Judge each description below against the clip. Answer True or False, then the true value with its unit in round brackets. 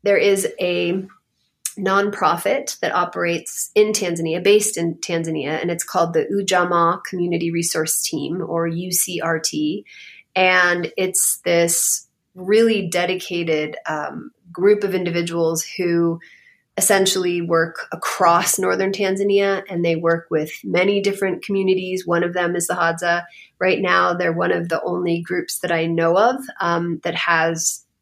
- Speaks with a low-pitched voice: False (175 Hz)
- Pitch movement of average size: False (2.3 semitones)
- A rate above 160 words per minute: False (135 wpm)